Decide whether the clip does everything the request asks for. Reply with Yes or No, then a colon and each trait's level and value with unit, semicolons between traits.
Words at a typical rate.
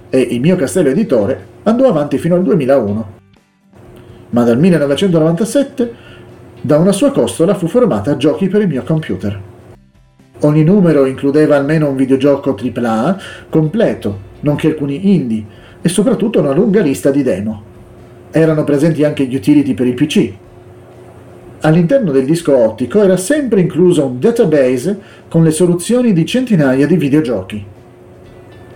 Yes: average, 140 wpm